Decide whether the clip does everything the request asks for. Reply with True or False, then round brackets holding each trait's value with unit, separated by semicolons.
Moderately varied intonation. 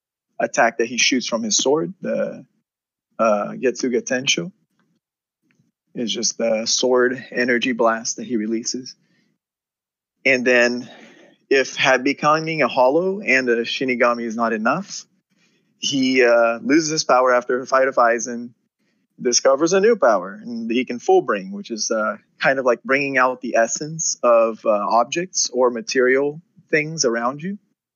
False (7.8 semitones)